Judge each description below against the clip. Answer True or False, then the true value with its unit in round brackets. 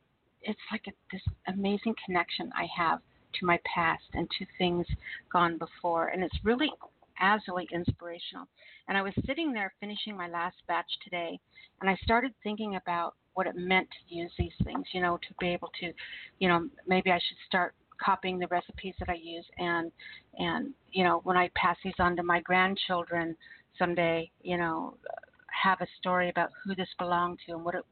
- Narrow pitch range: True (2.0 semitones)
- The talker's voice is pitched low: False (180 Hz)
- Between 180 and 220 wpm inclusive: True (185 wpm)